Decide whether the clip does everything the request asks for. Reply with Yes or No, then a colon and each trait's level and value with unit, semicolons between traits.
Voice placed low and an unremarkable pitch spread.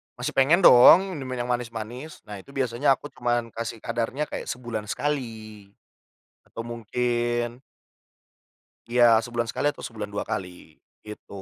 No: low, 120 Hz; narrow, 2.3 semitones